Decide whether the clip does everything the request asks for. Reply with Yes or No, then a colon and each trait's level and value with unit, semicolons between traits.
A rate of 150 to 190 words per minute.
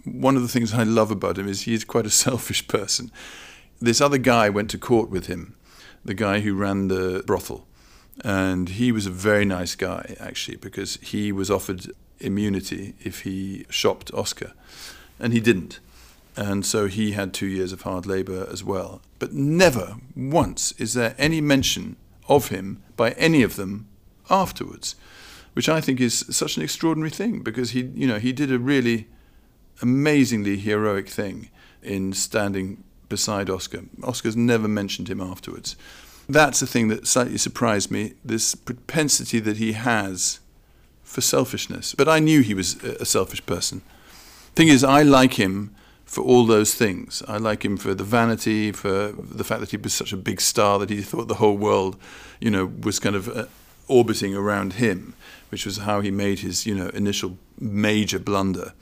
Yes: average, 180 wpm